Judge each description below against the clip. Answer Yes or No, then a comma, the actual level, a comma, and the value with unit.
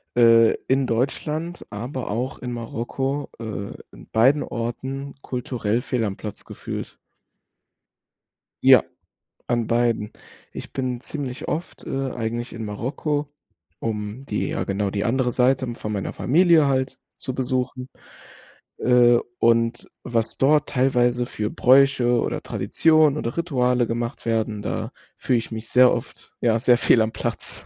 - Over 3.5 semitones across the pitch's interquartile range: No, average, 2.7 semitones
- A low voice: Yes, low, 125 Hz